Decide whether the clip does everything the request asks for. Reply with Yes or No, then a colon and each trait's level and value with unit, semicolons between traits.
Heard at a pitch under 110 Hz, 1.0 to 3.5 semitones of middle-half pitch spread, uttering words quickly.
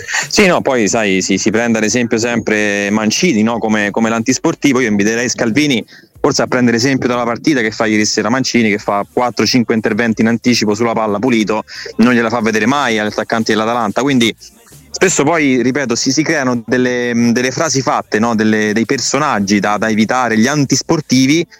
No: low, 115 Hz; narrow, 2.6 semitones; fast, 185 wpm